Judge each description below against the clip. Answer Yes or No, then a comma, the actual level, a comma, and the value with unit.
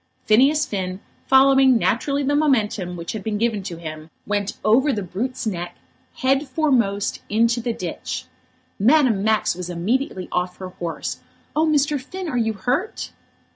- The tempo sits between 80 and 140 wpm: No, average, 155 wpm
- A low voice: No, high, 225 Hz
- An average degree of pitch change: No, wide, 6.1 semitones